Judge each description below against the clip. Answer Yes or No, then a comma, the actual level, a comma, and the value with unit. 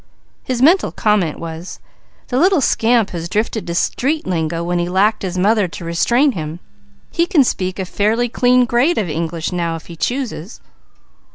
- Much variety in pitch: Yes, wide, 6.4 semitones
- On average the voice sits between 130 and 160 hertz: No, high, 200 Hz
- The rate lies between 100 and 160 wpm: No, average, 175 wpm